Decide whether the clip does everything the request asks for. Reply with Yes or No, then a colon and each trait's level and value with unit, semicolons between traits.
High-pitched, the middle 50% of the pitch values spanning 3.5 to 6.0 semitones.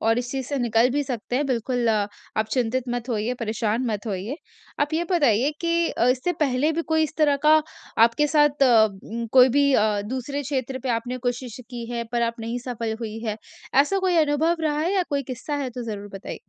Yes: very high, 250 Hz; average, 4.1 semitones